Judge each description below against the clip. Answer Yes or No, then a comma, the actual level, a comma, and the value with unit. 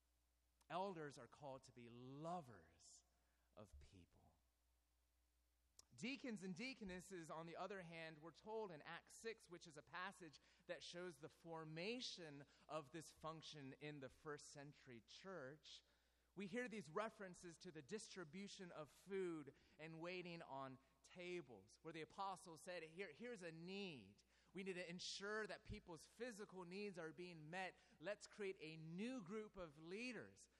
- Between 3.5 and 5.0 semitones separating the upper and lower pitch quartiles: No, wide, 5.4 semitones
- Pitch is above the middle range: No, medium, 165 Hz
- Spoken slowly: No, average, 145 wpm